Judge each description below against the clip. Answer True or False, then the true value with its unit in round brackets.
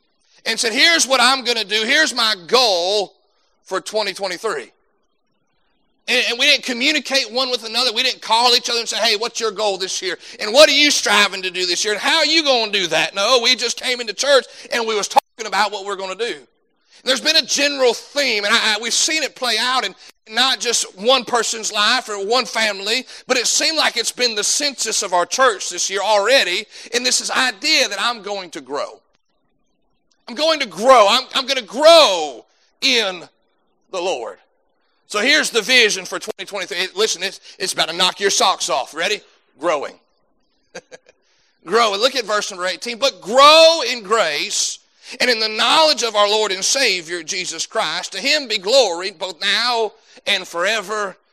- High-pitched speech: True (230 Hz)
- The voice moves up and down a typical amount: True (4.4 semitones)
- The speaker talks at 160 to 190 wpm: False (200 wpm)